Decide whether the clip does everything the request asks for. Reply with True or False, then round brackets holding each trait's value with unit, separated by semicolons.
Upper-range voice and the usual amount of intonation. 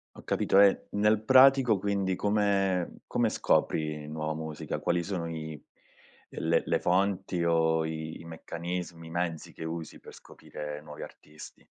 False (85 Hz; 3.6 semitones)